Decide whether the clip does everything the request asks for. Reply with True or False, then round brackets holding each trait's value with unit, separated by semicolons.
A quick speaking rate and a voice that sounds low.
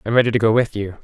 True (345 wpm; 110 Hz)